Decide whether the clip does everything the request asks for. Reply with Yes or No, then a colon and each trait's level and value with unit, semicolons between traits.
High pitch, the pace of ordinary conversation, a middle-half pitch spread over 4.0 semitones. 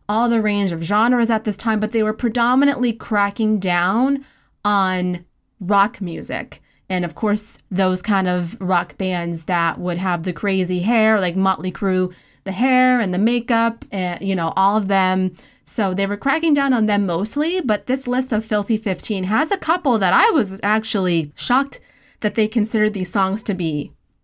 No: high, 205 Hz; average, 185 wpm; average, 3.6 semitones